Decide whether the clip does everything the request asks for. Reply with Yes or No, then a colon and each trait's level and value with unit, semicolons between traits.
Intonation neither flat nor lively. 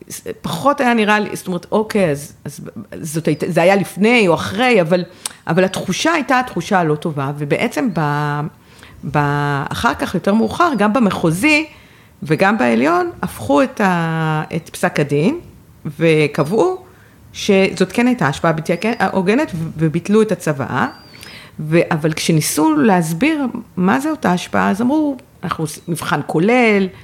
No: wide, 6.2 semitones